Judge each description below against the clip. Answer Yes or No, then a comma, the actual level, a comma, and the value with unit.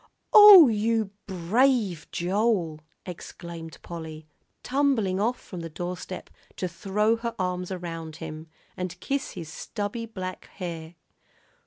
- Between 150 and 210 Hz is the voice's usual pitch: Yes, medium, 185 Hz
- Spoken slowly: Yes, slow, 120 wpm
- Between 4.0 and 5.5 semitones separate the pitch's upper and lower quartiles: Yes, average, 4.9 semitones